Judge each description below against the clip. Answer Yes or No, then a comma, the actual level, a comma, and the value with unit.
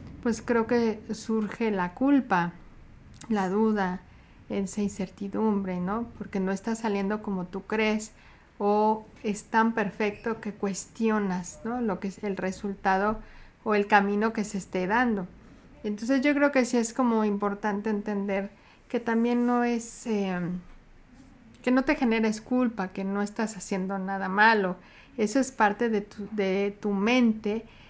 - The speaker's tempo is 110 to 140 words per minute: No, average, 150 wpm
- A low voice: No, high, 210 Hz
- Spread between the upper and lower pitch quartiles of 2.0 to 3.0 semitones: Yes, narrow, 2.4 semitones